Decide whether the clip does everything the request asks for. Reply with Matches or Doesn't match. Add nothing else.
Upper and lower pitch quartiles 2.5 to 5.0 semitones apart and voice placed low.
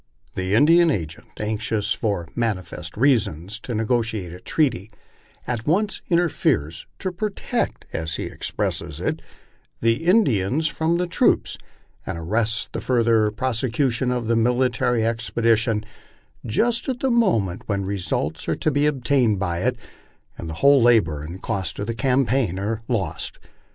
Doesn't match